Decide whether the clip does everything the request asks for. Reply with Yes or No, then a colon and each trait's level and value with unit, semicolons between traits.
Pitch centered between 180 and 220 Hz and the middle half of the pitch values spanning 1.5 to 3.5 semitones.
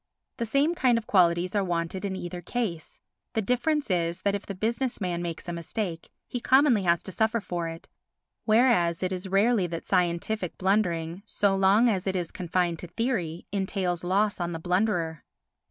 No: high, 190 Hz; average, 4.1 semitones